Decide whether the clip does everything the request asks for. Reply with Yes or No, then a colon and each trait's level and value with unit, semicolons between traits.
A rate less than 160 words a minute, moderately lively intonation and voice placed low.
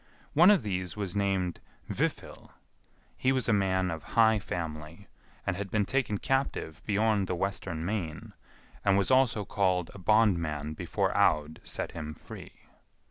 Yes: average, 150 wpm; average, 4.1 semitones; very low, 95 Hz